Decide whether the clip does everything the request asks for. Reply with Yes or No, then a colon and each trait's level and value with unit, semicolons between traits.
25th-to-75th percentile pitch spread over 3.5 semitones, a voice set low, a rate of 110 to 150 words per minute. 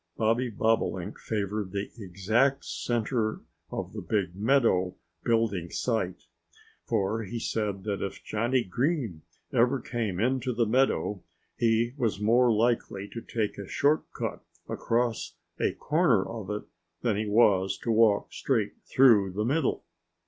No: average, 3.0 semitones; low, 110 Hz; average, 140 wpm